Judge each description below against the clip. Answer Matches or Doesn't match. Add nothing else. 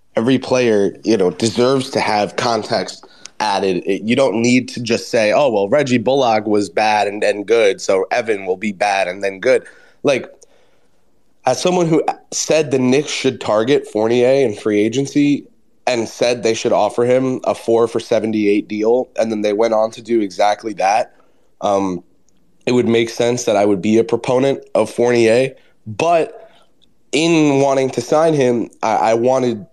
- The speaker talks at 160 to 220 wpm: Matches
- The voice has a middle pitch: Doesn't match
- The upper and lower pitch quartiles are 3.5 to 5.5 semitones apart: Matches